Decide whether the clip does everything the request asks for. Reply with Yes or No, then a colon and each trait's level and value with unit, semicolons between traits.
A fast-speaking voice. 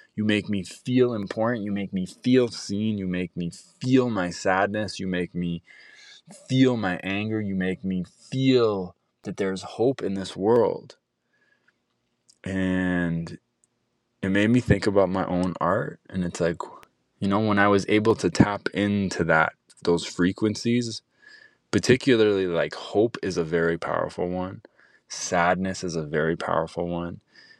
No: average, 150 wpm